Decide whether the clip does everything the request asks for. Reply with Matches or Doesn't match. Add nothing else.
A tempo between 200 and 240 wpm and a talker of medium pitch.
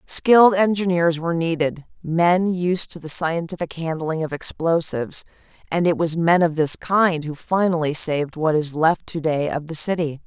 Doesn't match